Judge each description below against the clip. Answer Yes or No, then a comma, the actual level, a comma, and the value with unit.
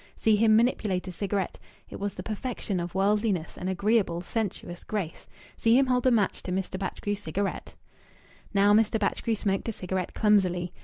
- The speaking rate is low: No, average, 170 wpm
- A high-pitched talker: Yes, high, 200 Hz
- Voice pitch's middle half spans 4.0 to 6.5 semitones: No, average, 2.9 semitones